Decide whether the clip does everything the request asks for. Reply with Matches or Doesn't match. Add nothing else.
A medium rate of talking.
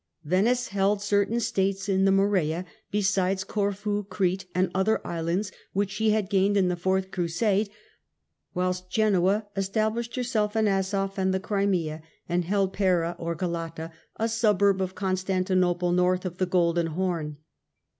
Matches